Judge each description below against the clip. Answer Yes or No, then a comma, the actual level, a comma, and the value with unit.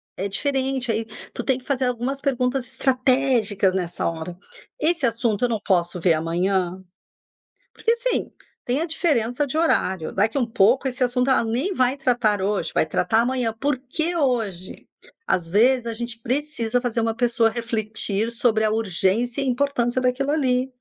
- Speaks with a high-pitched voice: Yes, high, 240 Hz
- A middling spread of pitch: Yes, average, 3.6 semitones